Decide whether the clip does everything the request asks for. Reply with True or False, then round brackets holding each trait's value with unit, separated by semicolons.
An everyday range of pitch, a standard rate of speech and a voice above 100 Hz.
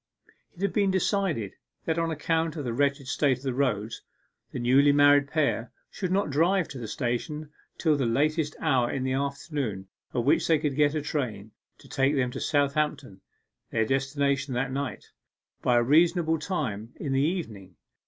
True (3.7 semitones; 180 wpm; 140 Hz)